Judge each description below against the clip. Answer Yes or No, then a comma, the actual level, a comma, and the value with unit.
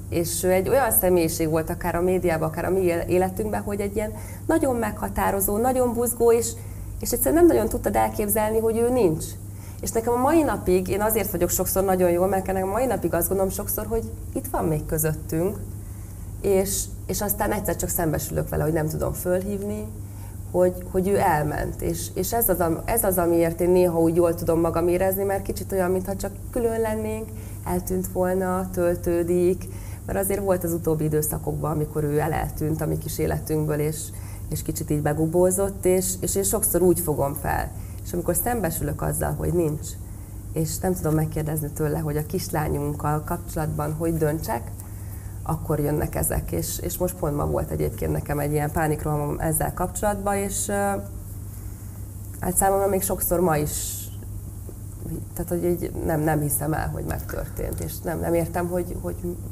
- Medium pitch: Yes, medium, 150 Hz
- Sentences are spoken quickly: Yes, fast, 175 wpm